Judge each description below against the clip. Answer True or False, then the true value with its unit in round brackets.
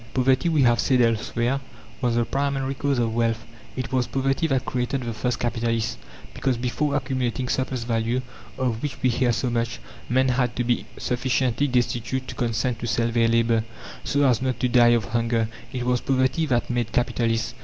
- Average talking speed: True (185 wpm)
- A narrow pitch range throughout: True (2.0 semitones)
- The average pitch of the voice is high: False (125 Hz)